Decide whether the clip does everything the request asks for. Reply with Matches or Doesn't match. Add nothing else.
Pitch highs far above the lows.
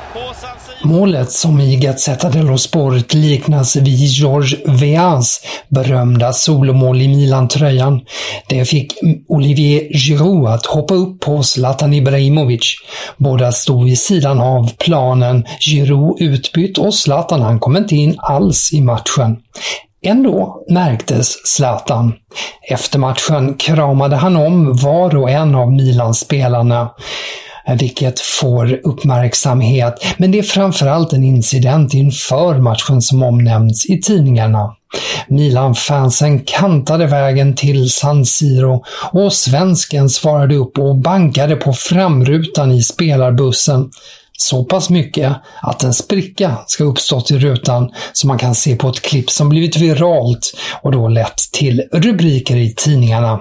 Doesn't match